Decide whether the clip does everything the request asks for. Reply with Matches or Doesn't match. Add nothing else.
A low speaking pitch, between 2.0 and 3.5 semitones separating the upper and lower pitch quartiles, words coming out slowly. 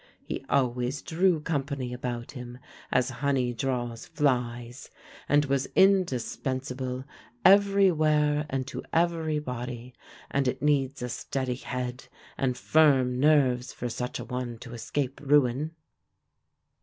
Matches